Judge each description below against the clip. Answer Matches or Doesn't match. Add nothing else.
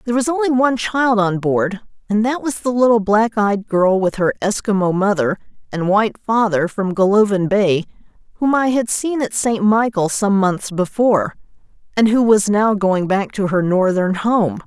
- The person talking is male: Doesn't match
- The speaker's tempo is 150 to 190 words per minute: Matches